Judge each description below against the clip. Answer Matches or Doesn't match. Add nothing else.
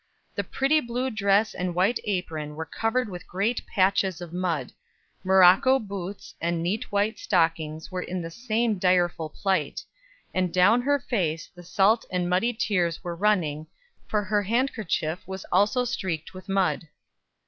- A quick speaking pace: Doesn't match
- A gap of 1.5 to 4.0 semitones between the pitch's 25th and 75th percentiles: Matches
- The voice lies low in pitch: Doesn't match